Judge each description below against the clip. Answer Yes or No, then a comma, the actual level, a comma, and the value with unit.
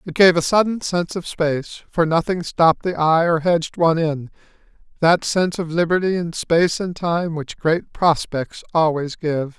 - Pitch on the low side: No, medium, 165 Hz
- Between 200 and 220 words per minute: No, average, 175 wpm